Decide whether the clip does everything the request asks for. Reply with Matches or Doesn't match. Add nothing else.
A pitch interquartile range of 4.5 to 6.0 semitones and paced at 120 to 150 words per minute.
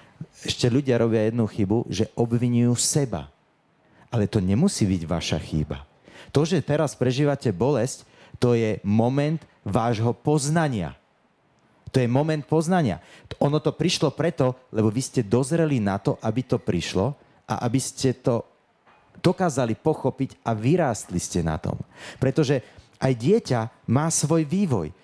Matches